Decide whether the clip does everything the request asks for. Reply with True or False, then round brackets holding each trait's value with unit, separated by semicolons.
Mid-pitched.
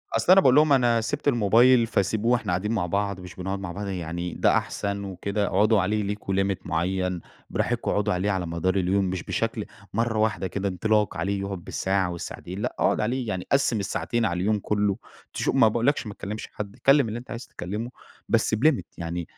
False (100 Hz)